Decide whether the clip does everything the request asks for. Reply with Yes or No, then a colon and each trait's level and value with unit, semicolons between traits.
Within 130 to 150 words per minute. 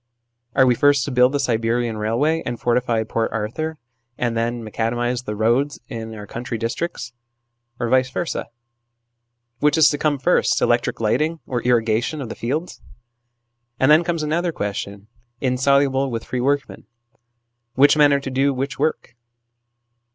No: average, 160 wpm